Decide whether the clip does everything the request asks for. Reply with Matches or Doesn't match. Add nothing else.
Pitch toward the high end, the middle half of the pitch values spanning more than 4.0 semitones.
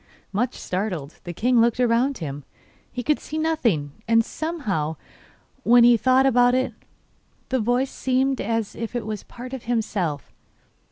Doesn't match